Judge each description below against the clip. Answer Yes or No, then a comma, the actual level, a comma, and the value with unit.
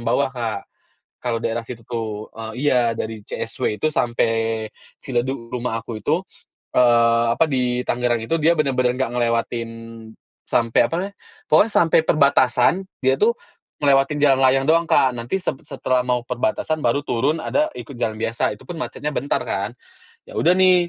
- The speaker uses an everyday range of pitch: Yes, average, 3.7 semitones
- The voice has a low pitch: Yes, low, 125 Hz